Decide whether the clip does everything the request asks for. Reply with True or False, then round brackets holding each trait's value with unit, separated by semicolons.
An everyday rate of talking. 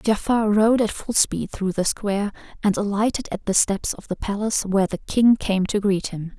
False (215 wpm)